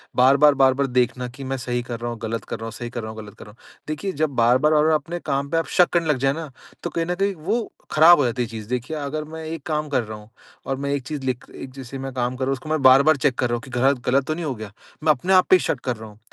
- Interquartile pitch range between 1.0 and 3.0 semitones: No, average, 4.0 semitones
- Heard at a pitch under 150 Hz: Yes, low, 135 Hz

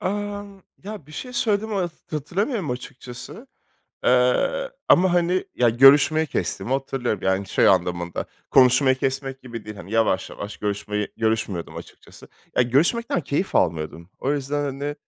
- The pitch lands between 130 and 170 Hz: Yes, low, 135 Hz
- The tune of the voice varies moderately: No, wide, 7.8 semitones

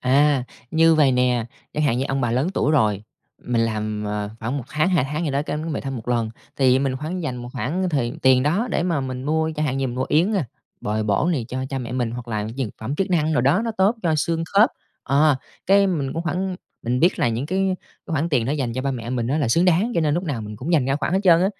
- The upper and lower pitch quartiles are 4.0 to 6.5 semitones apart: Yes, average, 5.0 semitones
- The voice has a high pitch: No, medium, 140 Hz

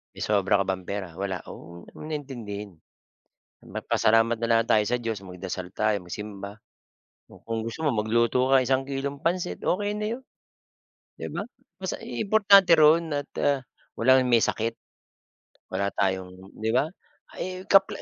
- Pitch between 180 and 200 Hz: No, low, 115 Hz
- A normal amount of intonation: No, wide, 6.2 semitones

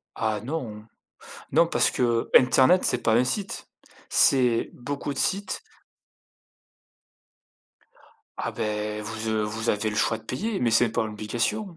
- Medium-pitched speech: No, low, 115 Hz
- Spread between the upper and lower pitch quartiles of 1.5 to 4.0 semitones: No, average, 4.6 semitones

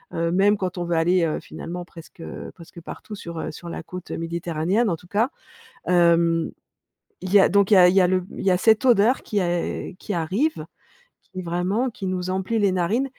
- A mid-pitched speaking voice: Yes, medium, 180 Hz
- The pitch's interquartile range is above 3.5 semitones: No, average, 3.0 semitones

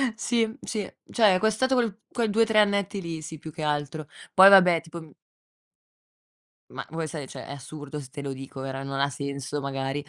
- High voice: No, medium, 160 Hz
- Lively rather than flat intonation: Yes, wide, 6.5 semitones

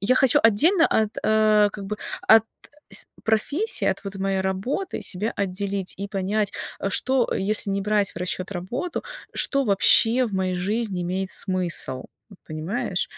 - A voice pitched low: No, high, 200 Hz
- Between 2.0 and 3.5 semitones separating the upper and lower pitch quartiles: Yes, average, 2.9 semitones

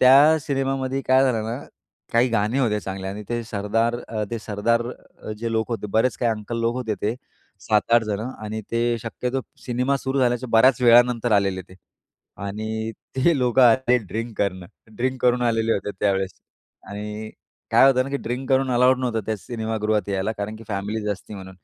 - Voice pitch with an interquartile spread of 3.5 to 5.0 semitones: No, average, 3.0 semitones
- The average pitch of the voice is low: Yes, low, 115 Hz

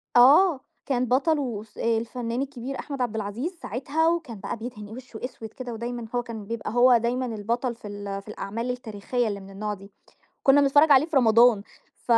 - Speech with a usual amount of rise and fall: Yes, average, 3.1 semitones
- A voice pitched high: Yes, high, 240 Hz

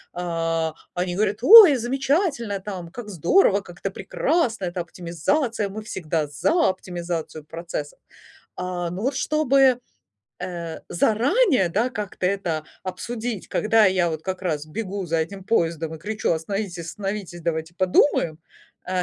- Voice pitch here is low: No, medium, 185 Hz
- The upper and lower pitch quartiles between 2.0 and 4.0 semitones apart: No, average, 5.0 semitones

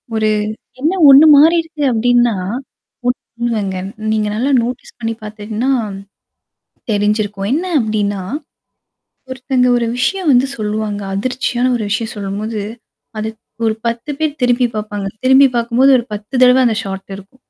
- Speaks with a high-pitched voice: Yes, high, 235 Hz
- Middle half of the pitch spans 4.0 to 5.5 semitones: No, average, 3.4 semitones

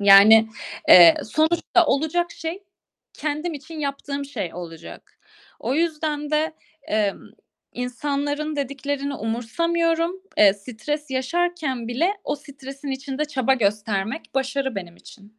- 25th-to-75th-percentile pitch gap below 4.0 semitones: No, wide, 5.6 semitones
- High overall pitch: Yes, very high, 280 Hz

